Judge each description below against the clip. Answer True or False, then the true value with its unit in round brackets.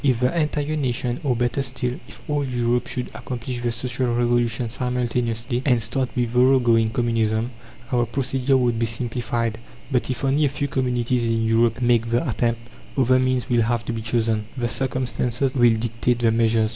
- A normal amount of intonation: False (1.8 semitones)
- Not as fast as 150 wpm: False (185 wpm)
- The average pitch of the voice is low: True (120 Hz)